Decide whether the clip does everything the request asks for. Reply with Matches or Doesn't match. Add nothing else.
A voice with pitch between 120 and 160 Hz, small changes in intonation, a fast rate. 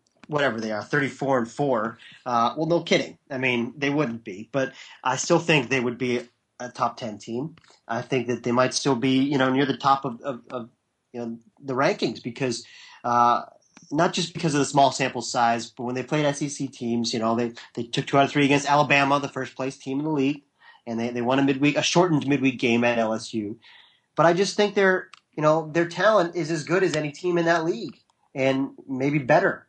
Doesn't match